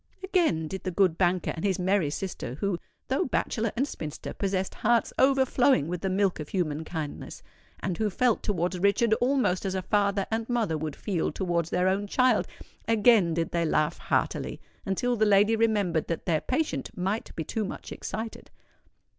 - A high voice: Yes, high, 195 Hz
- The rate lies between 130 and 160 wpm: No, average, 170 wpm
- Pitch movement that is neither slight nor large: Yes, average, 4.6 semitones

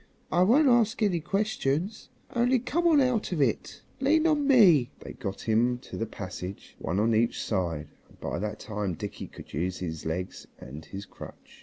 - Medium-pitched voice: No, low, 125 Hz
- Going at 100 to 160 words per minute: No, average, 190 wpm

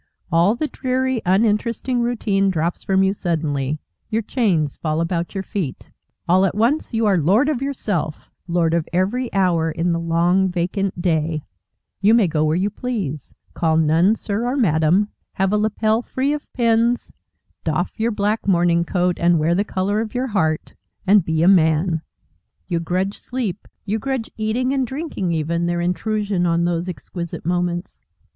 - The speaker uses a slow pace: No, average, 170 wpm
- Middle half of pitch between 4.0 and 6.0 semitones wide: Yes, average, 4.6 semitones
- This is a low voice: No, high, 190 Hz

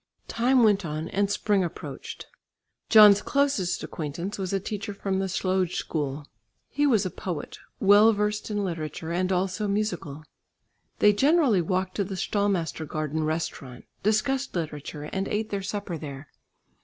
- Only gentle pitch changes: No, average, 4.3 semitones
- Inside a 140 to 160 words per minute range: Yes, average, 145 wpm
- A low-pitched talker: No, high, 190 Hz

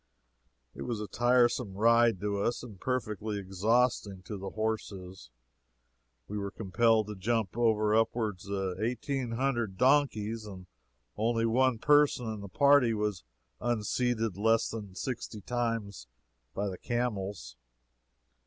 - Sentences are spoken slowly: Yes, slow, 130 wpm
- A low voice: Yes, low, 110 Hz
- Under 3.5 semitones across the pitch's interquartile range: Yes, average, 3.1 semitones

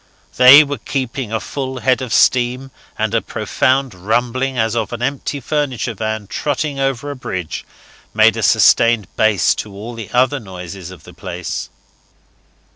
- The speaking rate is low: No, average, 160 wpm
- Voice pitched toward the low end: Yes, low, 120 Hz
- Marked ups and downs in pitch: No, average, 4.0 semitones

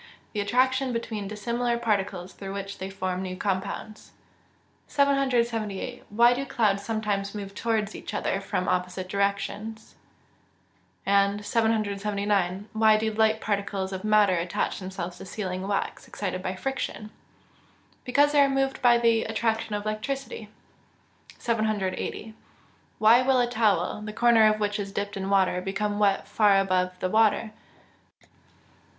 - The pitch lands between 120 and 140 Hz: No, high, 210 Hz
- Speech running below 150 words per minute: Yes, average, 140 wpm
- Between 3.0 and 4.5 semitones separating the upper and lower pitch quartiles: No, narrow, 2.6 semitones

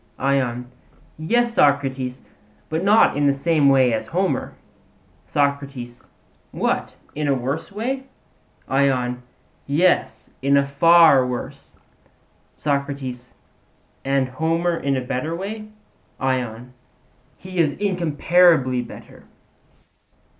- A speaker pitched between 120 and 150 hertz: Yes, medium, 140 Hz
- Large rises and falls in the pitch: No, average, 4.4 semitones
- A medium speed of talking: No, slow, 105 wpm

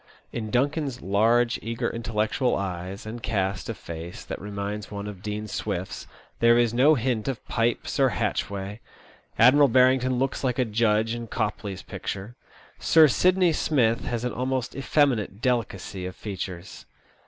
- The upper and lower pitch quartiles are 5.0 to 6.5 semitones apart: No, average, 3.8 semitones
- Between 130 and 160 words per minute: Yes, average, 150 wpm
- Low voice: Yes, low, 115 Hz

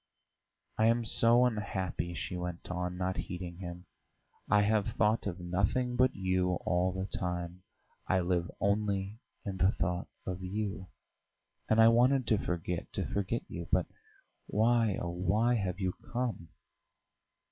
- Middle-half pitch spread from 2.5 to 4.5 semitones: Yes, average, 3.5 semitones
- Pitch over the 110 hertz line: No, very low, 95 Hz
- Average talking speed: Yes, average, 145 wpm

